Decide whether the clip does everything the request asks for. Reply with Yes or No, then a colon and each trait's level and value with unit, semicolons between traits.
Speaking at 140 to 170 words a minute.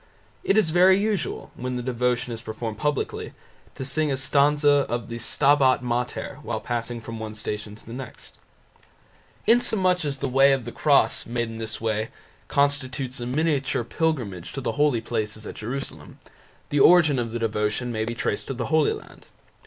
No: average, 180 wpm